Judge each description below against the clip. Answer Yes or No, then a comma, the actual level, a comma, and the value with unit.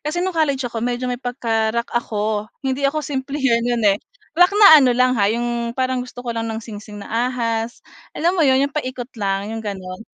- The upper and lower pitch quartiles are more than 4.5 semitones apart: No, average, 3.2 semitones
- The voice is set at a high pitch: Yes, high, 245 Hz